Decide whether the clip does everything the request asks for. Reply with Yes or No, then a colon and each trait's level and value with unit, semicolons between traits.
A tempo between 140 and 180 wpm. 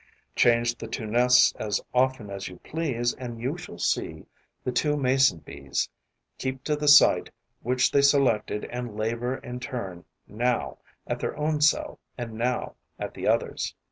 Yes: average, 165 wpm